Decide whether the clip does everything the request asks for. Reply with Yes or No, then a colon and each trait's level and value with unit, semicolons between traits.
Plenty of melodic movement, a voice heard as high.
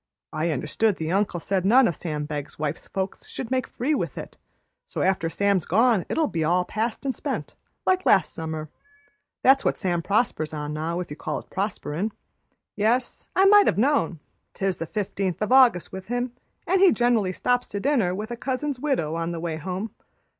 Yes: wide, 6.8 semitones; high, 195 Hz